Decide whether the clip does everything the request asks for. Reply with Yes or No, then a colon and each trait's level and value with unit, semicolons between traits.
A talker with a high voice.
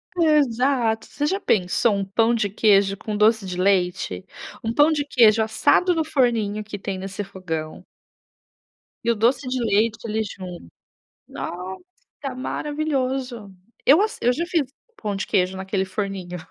Yes: high, 220 Hz